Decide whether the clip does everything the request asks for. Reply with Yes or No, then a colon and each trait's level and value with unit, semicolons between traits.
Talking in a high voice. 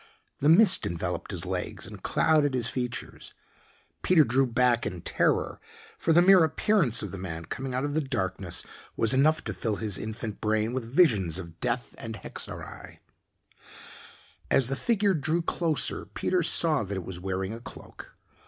No: low, 125 Hz